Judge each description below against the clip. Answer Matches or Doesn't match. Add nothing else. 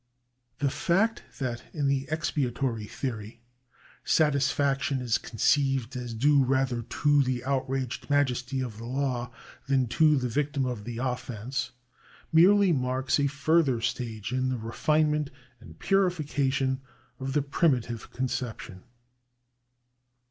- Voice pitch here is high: Doesn't match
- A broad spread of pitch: Doesn't match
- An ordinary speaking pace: Doesn't match